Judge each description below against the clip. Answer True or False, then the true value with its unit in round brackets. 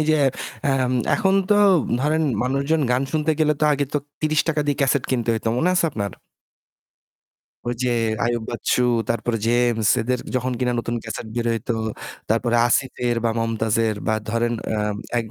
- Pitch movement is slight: False (3.6 semitones)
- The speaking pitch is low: True (125 Hz)